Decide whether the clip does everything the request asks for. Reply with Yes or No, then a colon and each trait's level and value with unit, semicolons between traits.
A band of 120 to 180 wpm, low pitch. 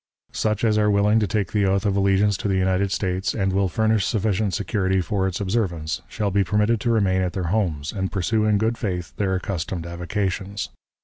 No: fast, 205 wpm; low, 100 Hz